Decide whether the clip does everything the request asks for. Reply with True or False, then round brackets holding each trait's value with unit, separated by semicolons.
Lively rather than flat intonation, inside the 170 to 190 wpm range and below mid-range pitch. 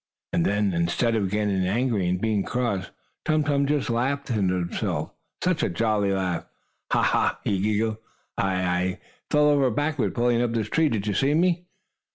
True (6.3 semitones; 175 wpm; 110 Hz)